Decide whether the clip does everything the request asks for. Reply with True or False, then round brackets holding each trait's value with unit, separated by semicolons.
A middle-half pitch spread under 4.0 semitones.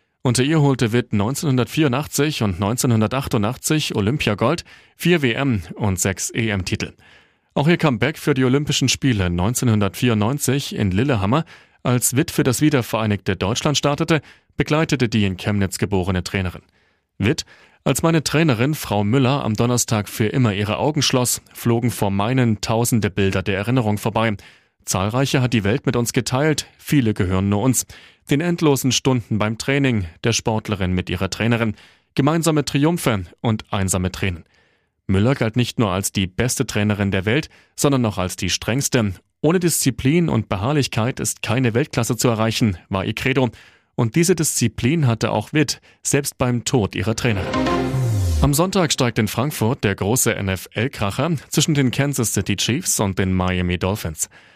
False (5.0 semitones)